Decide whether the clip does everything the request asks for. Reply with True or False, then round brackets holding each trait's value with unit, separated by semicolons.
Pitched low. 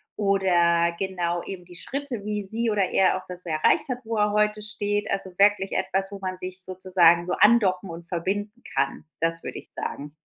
False (190 Hz)